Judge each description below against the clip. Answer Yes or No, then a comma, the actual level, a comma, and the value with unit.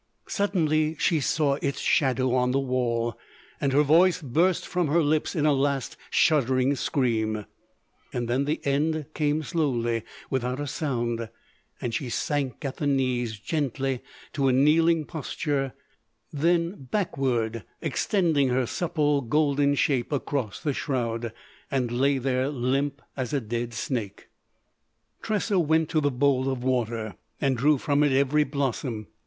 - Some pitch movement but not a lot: Yes, average, 3.3 semitones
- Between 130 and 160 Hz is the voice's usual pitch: Yes, medium, 140 Hz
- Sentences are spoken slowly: No, average, 145 wpm